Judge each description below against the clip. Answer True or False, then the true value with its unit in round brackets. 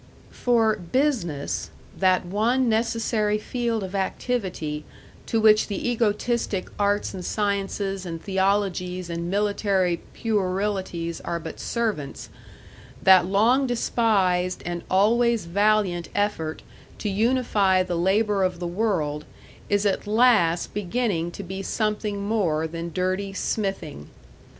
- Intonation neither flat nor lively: True (3.4 semitones)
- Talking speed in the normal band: False (115 wpm)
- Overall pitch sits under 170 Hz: False (200 Hz)